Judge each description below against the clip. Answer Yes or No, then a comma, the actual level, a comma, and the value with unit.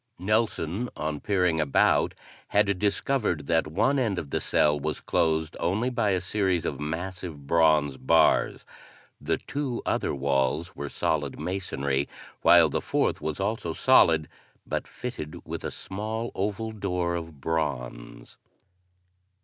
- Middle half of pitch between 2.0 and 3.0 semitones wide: No, average, 5.1 semitones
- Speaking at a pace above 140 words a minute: No, slow, 135 wpm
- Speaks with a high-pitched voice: No, very low, 85 Hz